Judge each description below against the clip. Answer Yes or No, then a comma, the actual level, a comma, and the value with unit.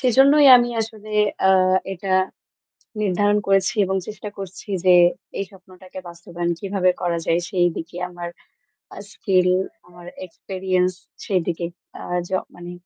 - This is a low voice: No, medium, 185 Hz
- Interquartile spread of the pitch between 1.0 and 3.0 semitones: Yes, narrow, 2.5 semitones